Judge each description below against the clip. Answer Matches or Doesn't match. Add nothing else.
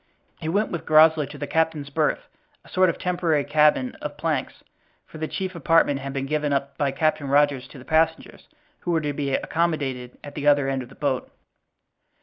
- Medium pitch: Matches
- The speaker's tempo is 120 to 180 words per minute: Doesn't match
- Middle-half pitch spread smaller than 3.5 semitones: Matches